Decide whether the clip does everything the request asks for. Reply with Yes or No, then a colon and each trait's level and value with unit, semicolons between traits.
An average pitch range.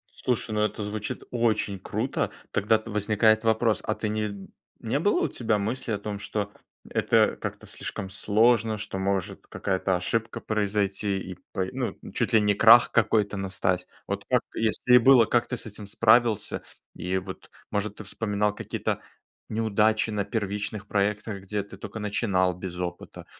No: narrow, 1.9 semitones